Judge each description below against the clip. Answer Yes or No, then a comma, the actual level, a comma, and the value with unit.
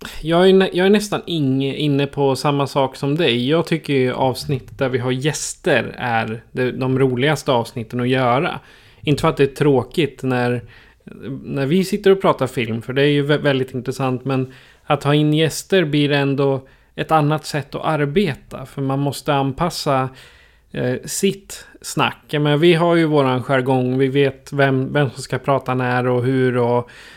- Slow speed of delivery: No, average, 180 wpm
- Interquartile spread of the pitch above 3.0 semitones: No, average, 2.7 semitones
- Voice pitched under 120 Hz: No, medium, 140 Hz